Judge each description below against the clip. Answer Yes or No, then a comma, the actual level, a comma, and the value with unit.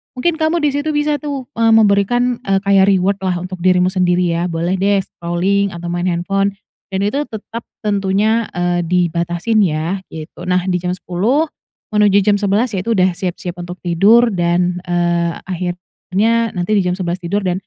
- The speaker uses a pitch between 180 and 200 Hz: Yes, high, 190 Hz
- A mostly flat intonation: No, average, 3.2 semitones